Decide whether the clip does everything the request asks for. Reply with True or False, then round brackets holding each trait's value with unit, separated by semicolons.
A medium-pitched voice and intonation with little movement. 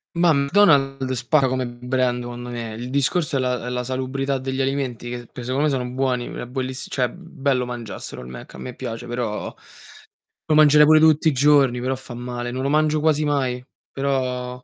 False (130 Hz; 2.3 semitones)